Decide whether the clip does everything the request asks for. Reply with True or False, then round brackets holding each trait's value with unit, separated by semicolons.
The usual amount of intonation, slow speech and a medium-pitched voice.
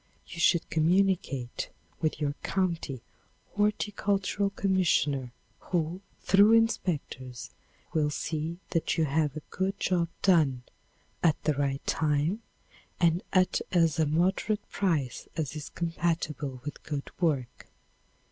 True (4.2 semitones; 115 wpm; 165 Hz)